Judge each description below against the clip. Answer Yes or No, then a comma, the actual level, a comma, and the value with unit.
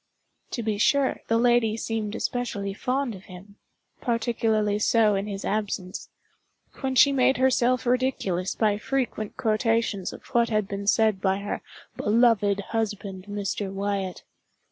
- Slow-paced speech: Yes, slow, 130 wpm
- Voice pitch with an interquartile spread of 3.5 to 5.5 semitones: No, average, 3.0 semitones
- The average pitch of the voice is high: Yes, high, 215 Hz